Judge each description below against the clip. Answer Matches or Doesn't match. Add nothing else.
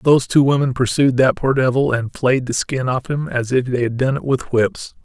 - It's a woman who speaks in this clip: Doesn't match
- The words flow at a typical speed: Doesn't match